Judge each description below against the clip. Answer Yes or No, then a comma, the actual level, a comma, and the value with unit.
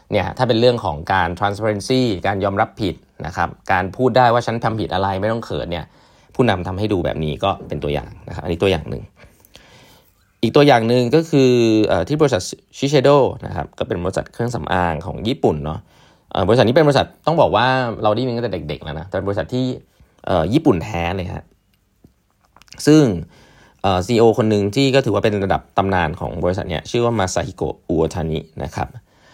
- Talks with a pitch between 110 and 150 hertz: No, low, 100 Hz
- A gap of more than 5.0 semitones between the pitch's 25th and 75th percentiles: Yes, wide, 5.4 semitones